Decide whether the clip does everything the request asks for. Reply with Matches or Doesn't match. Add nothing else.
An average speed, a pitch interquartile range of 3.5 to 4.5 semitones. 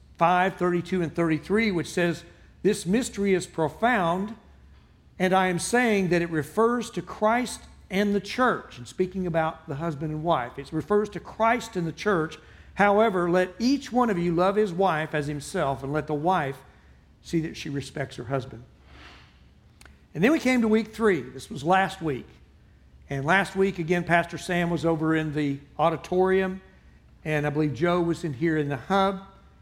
Matches